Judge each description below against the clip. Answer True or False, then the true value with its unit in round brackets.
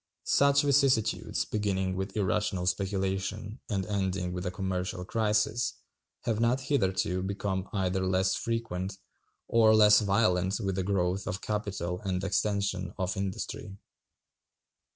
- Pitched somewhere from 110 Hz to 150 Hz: False (95 Hz)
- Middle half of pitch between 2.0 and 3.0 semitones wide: True (2.4 semitones)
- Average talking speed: False (125 wpm)